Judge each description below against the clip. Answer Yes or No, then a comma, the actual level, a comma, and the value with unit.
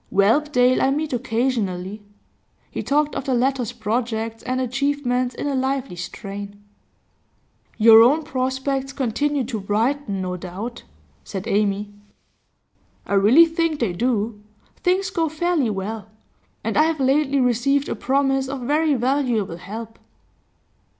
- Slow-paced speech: Yes, slow, 130 wpm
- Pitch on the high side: Yes, very high, 250 Hz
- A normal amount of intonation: Yes, average, 4.6 semitones